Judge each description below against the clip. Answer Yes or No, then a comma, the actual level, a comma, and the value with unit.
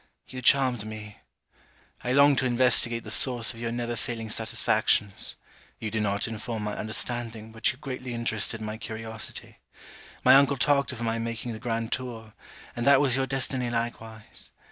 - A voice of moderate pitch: No, low, 115 Hz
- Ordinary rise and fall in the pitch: No, narrow, 2.3 semitones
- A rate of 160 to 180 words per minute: Yes, average, 165 wpm